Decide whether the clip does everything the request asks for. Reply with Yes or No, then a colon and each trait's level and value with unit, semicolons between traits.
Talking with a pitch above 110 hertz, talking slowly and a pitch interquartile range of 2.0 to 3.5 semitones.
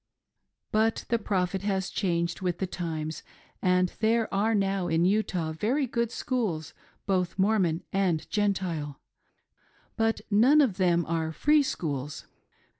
No: high, 190 Hz; slow, 130 wpm; average, 4.3 semitones